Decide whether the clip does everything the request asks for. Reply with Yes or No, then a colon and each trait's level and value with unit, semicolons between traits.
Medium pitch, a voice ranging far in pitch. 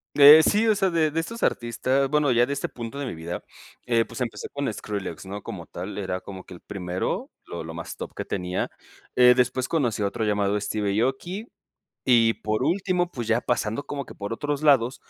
No: low, 120 Hz; wide, 5.7 semitones